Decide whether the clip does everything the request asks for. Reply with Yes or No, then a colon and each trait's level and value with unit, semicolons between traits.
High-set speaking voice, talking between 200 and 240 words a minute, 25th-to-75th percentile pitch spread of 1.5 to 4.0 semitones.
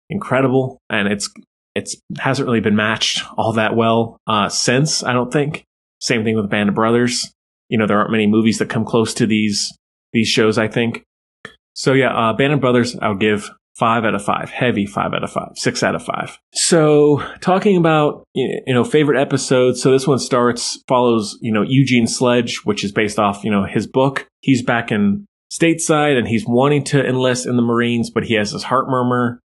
No: low, 120 Hz; fast, 205 wpm; average, 3.4 semitones